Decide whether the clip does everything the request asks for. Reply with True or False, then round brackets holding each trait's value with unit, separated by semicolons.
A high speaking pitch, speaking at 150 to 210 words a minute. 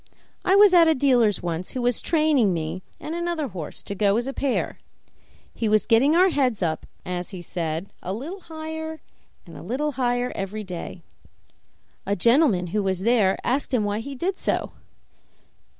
True (240 Hz; 180 wpm)